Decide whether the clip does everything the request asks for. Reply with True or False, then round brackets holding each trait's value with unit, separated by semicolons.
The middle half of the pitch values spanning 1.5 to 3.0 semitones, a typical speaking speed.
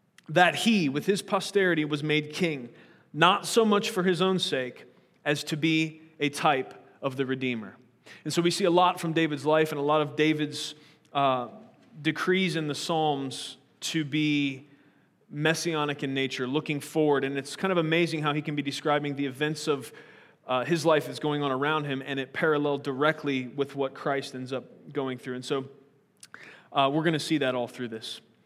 True (2.7 semitones; 195 wpm)